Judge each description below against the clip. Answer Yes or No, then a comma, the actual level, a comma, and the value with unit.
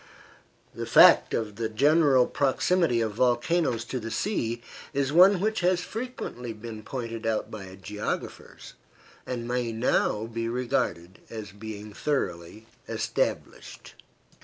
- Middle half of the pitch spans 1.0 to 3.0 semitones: No, average, 4.3 semitones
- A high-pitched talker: No, low, 115 Hz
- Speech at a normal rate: No, slow, 125 wpm